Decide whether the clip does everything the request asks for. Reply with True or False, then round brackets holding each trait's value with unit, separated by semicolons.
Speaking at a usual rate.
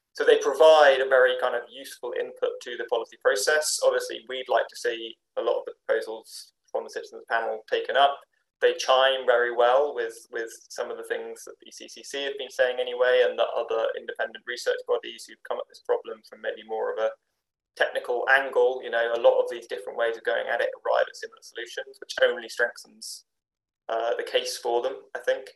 False (210 wpm)